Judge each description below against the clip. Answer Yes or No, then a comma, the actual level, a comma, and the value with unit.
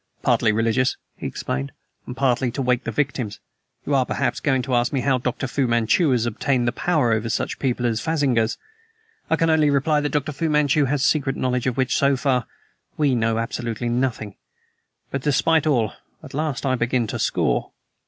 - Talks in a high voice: No, low, 130 Hz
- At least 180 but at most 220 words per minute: Yes, average, 190 wpm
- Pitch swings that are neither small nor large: Yes, average, 3.2 semitones